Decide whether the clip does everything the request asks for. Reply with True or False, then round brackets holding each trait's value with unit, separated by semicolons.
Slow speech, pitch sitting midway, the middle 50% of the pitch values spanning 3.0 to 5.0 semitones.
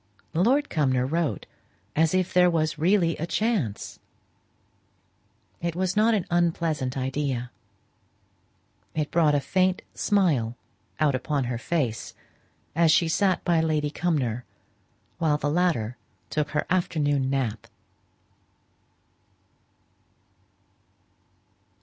True (105 wpm; 155 Hz; 4.3 semitones)